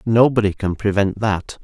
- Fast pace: No, average, 145 wpm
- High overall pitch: No, low, 105 Hz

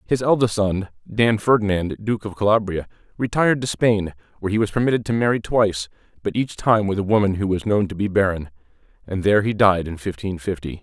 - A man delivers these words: Yes, male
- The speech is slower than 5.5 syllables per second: No, 5.9 syllables/s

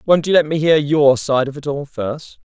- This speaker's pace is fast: Yes, fast, 260 wpm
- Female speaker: No, male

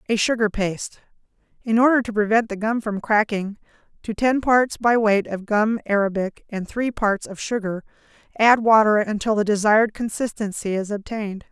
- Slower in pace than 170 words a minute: Yes, average, 160 wpm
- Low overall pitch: No, high, 215 Hz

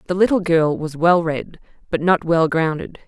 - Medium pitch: Yes, medium, 170 Hz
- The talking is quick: No, average, 195 wpm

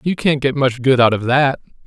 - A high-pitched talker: No, low, 135 Hz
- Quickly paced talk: Yes, fast, 260 wpm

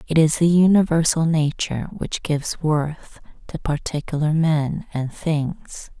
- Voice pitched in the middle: Yes, medium, 155 Hz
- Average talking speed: No, slow, 130 wpm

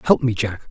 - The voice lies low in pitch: Yes, low, 120 Hz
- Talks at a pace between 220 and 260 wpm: Yes, fast, 255 wpm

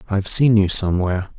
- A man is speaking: Yes, male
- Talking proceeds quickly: Yes, fast, 215 wpm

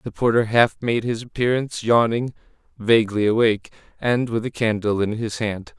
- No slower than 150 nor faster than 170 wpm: Yes, average, 165 wpm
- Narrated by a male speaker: Yes, male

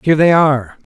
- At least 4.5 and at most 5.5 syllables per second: No, 7.0 syllables/s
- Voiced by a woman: No, male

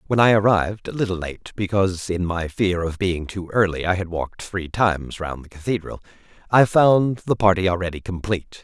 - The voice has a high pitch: No, very low, 95 Hz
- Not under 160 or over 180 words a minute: No, average, 195 wpm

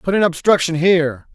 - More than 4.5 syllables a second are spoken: Yes, 5.5 syllables/s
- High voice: No, medium, 170 Hz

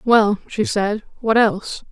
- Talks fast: No, average, 155 wpm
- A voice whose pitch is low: No, high, 215 Hz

